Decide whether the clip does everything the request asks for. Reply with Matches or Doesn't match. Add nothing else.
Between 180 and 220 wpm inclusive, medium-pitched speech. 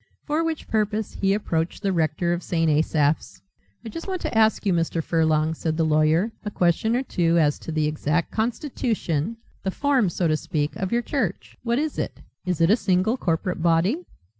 Matches